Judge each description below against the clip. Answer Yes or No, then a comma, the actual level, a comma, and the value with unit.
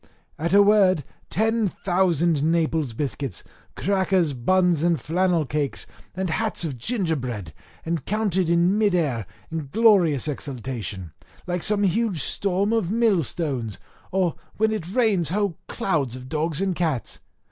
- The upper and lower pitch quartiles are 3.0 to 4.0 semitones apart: No, average, 5.1 semitones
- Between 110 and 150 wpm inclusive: Yes, average, 140 wpm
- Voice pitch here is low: No, medium, 170 Hz